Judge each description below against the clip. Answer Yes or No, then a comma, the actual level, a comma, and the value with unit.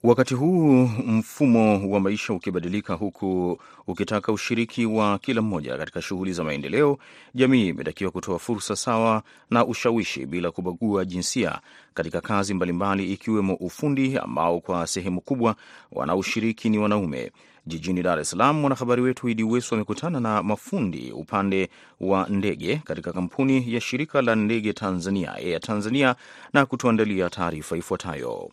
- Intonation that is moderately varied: Yes, average, 4.3 semitones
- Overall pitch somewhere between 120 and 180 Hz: No, low, 105 Hz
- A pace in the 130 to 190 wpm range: Yes, average, 135 wpm